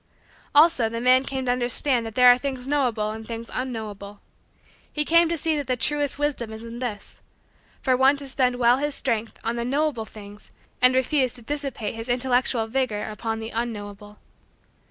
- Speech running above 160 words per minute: Yes, average, 180 wpm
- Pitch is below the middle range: No, high, 245 Hz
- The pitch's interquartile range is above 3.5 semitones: No, average, 3.2 semitones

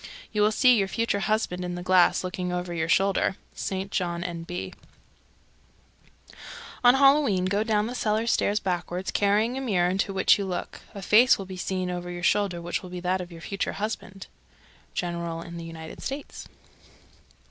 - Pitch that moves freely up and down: No, average, 3.0 semitones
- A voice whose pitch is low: No, medium, 185 Hz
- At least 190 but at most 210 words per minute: No, average, 180 wpm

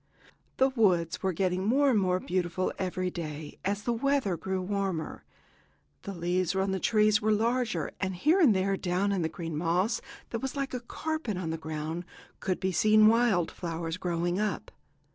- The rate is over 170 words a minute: Yes, average, 180 wpm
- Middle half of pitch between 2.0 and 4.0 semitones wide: Yes, average, 3.7 semitones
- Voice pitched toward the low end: No, high, 190 Hz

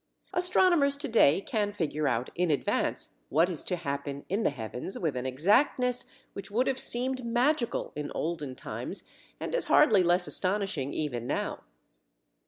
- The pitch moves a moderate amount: No, wide, 9.0 semitones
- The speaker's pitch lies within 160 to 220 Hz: Yes, medium, 185 Hz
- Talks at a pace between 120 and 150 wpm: No, average, 160 wpm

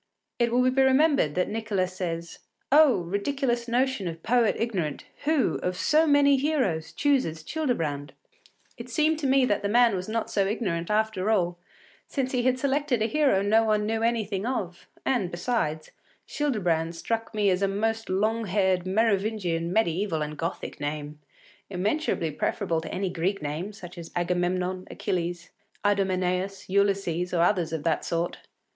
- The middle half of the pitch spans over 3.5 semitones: Yes, average, 5.3 semitones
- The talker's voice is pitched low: No, high, 200 Hz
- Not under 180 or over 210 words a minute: No, average, 160 wpm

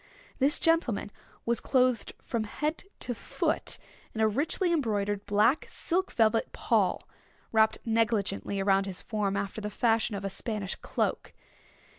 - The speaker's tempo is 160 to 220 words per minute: No, average, 140 wpm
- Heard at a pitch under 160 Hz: No, high, 220 Hz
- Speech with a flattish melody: No, average, 3.5 semitones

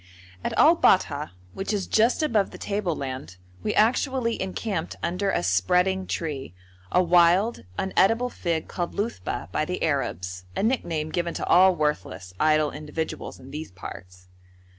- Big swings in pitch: Yes, wide, 5.9 semitones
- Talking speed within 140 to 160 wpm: Yes, average, 145 wpm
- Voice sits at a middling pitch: Yes, medium, 170 Hz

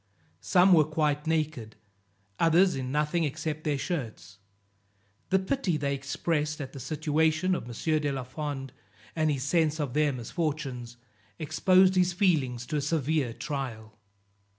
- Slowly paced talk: No, average, 145 wpm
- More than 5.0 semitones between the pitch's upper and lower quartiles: No, average, 3.2 semitones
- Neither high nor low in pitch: Yes, medium, 150 Hz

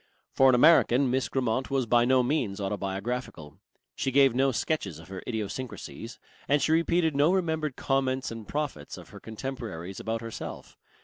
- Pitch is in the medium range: No, low, 125 Hz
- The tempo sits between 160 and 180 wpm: Yes, average, 165 wpm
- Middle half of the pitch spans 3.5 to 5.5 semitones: Yes, average, 3.9 semitones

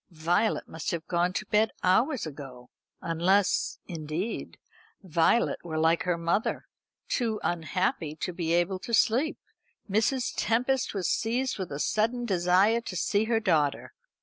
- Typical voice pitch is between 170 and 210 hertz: Yes, medium, 185 Hz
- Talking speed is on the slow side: No, average, 145 wpm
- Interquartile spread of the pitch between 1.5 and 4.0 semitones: No, average, 5.0 semitones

